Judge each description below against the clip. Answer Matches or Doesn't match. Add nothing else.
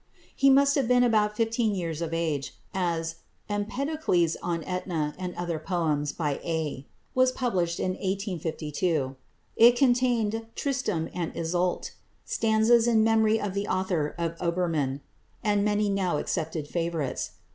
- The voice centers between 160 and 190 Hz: Matches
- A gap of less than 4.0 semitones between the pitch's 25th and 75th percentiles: Doesn't match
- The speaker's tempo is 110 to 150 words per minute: Matches